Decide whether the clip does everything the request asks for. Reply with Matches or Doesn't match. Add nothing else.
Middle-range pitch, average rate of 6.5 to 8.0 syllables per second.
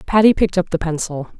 Matches